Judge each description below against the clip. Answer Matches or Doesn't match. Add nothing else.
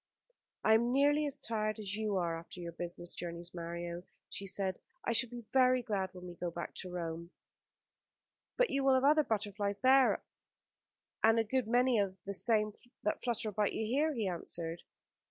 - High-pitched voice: Matches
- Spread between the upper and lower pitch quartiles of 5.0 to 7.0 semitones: Matches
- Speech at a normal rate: Matches